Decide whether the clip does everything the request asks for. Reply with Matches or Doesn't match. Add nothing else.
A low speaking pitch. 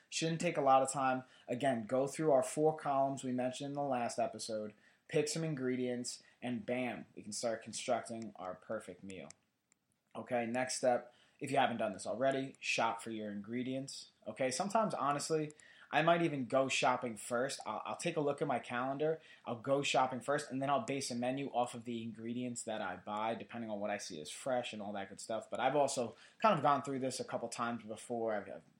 Matches